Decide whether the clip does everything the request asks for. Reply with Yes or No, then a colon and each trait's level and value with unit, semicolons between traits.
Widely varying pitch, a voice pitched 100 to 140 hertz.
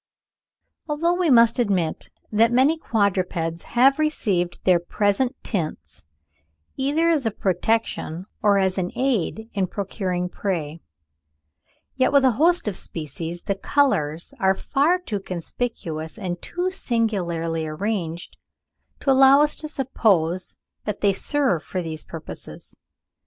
No: wide, 7.2 semitones; high, 205 Hz